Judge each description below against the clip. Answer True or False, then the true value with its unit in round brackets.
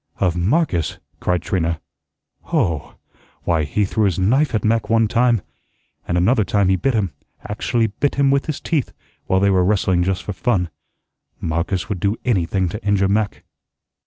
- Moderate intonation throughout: True (4.2 semitones)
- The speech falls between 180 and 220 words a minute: False (170 wpm)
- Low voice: True (100 Hz)